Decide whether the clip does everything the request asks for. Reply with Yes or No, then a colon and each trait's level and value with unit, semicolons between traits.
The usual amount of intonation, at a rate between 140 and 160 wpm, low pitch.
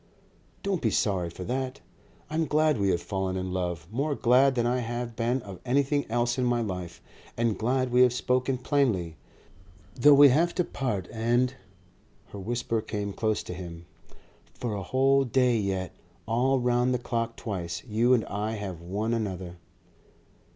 No: average, 4.7 semitones; average, 175 wpm; low, 115 Hz